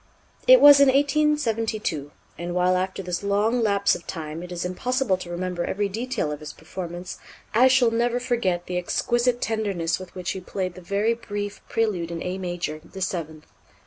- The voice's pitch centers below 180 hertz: No, high, 190 Hz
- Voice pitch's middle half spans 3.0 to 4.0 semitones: No, average, 4.8 semitones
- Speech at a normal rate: Yes, average, 180 wpm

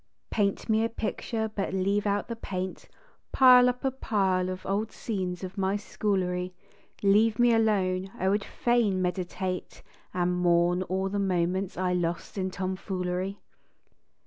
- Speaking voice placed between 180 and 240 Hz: Yes, high, 190 Hz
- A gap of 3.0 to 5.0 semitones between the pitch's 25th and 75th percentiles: No, narrow, 2.5 semitones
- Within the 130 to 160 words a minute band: Yes, average, 150 wpm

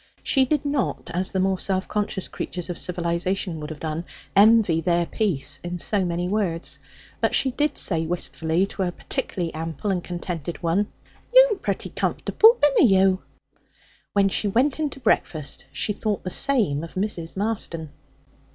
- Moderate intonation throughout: Yes, average, 4.1 semitones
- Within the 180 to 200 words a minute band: No, average, 165 wpm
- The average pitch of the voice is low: No, medium, 185 Hz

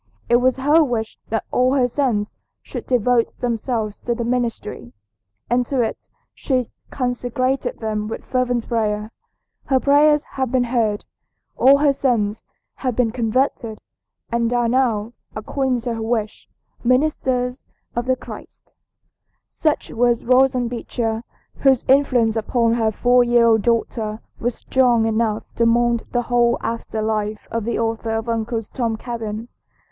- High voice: Yes, high, 240 Hz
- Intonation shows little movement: Yes, narrow, 2.2 semitones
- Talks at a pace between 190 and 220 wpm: No, average, 145 wpm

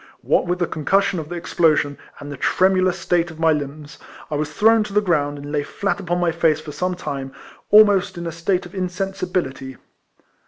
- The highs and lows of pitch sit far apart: No, average, 3.8 semitones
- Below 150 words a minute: No, average, 200 wpm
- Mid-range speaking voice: Yes, medium, 175 Hz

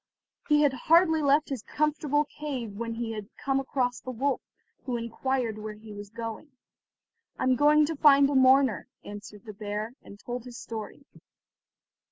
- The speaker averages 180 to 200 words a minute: No, average, 170 wpm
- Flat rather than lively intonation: No, average, 4.4 semitones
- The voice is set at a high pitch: Yes, very high, 255 Hz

